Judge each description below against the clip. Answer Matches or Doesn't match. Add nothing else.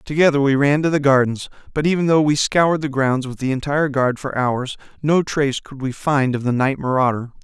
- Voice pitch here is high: Doesn't match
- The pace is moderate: Doesn't match